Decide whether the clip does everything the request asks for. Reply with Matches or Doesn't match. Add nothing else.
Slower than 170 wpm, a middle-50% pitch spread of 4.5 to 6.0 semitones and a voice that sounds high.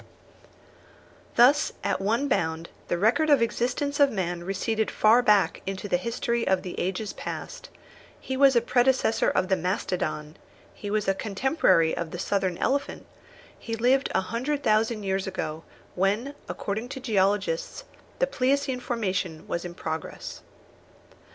Matches